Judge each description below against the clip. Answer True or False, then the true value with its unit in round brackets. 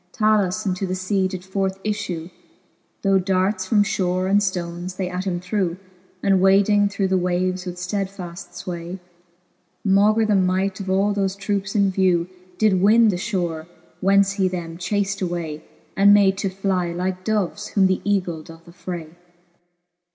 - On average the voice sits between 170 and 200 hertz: True (190 Hz)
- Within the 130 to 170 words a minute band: True (160 wpm)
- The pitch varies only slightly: True (1.8 semitones)